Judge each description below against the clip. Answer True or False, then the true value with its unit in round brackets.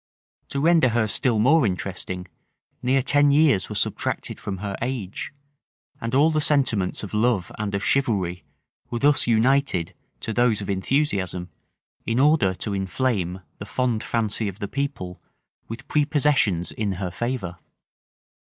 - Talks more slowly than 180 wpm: True (145 wpm)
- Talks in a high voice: False (115 Hz)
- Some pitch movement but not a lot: False (5.9 semitones)